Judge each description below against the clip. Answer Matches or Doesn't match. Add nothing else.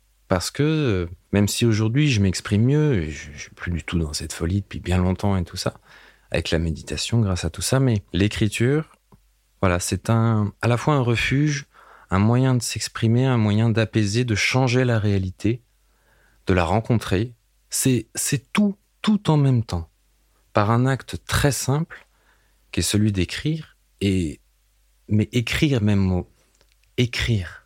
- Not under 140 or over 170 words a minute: Matches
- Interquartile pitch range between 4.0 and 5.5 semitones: Matches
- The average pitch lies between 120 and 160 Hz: Doesn't match